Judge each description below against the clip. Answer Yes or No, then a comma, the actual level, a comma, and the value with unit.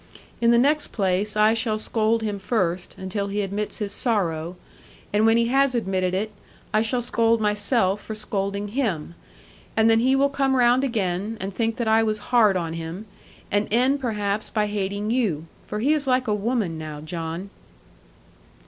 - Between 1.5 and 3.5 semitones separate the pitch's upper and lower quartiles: Yes, average, 3.2 semitones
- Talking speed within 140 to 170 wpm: No, average, 180 wpm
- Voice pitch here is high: Yes, high, 215 Hz